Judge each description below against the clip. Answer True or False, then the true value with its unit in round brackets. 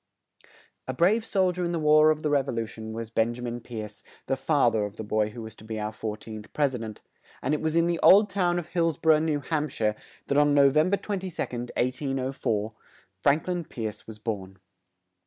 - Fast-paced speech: True (235 wpm)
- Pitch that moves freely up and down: True (6.3 semitones)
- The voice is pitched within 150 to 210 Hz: False (135 Hz)